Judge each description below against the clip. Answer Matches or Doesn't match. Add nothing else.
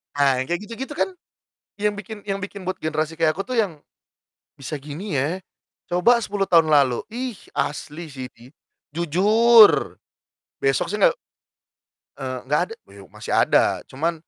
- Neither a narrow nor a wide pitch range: Doesn't match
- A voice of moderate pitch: Matches